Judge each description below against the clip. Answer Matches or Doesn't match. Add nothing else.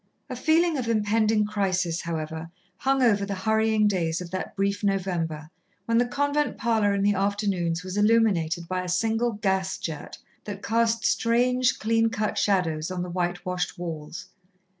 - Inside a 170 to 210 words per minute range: Doesn't match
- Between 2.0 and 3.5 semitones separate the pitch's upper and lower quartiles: Doesn't match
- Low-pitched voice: Doesn't match